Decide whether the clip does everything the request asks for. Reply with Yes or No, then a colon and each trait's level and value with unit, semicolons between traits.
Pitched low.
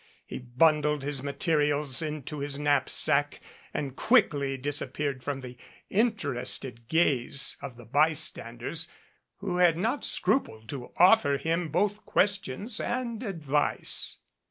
No: medium, 150 Hz